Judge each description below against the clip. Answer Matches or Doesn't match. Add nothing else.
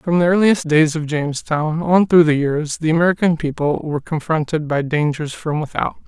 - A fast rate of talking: Doesn't match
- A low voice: Doesn't match